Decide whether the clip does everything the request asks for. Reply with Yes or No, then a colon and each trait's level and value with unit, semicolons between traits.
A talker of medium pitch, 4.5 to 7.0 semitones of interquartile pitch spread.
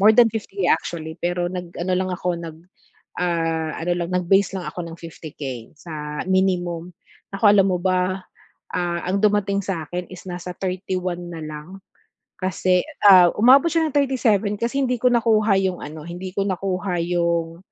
No: medium, 180 Hz; narrow, 2.4 semitones